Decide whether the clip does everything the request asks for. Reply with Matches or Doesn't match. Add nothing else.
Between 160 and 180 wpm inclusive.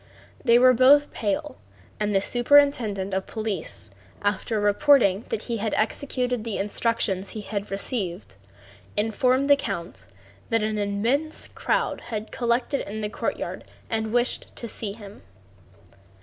Doesn't match